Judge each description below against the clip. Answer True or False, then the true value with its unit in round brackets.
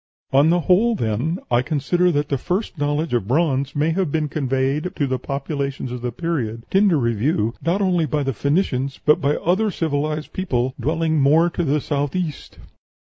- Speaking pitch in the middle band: True (150 Hz)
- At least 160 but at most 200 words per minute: True (185 wpm)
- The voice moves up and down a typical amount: True (3.9 semitones)